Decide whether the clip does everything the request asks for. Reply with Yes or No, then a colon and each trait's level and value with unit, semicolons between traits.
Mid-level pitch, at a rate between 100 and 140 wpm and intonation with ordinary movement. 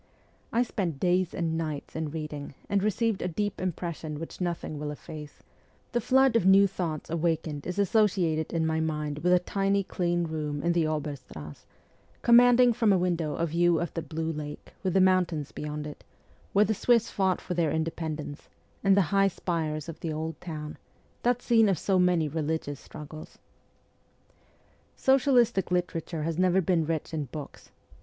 No: medium, 170 Hz; average, 175 wpm; average, 3.7 semitones